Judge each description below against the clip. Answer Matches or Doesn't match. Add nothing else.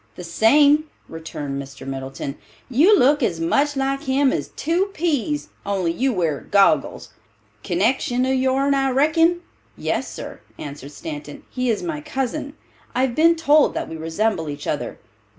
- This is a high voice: Matches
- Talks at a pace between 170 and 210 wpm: Doesn't match